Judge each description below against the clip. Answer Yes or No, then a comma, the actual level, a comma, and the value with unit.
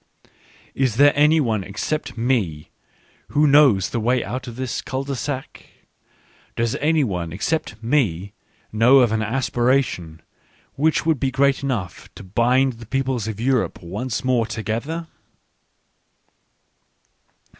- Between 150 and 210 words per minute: No, slow, 135 wpm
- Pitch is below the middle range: Yes, low, 125 Hz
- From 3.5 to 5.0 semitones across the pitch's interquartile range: Yes, average, 4.0 semitones